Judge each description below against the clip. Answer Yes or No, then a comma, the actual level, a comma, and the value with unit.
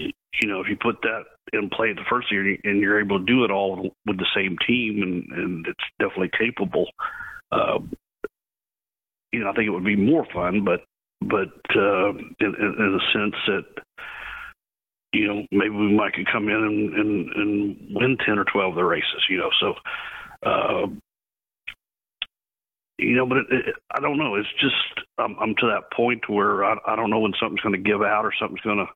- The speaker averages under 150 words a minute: No, fast, 205 wpm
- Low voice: Yes, low, 105 Hz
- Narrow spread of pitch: Yes, narrow, 2.0 semitones